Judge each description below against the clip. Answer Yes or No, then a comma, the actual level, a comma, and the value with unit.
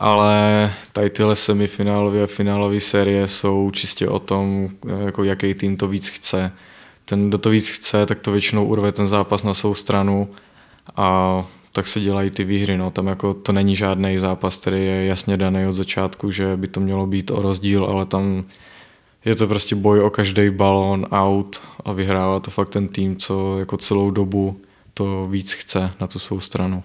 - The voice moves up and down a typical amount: No, narrow, 1.1 semitones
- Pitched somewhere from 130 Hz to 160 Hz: No, low, 100 Hz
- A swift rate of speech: Yes, fast, 190 wpm